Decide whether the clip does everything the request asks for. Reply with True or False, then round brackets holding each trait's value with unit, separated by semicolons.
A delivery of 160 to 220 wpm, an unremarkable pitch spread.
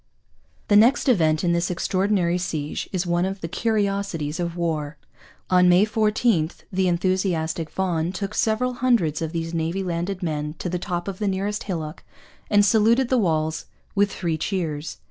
True (165 wpm; 3.5 semitones)